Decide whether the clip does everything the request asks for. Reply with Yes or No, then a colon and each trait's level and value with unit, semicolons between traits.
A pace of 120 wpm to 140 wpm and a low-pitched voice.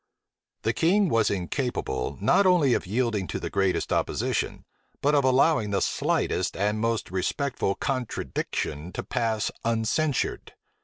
Yes: slow, 135 wpm; low, 115 Hz